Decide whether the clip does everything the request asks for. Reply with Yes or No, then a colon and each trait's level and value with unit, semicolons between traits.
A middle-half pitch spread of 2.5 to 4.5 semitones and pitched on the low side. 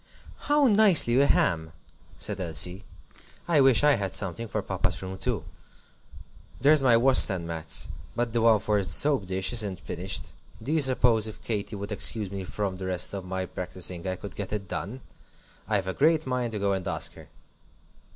No: average, 5.1 semitones; low, 105 Hz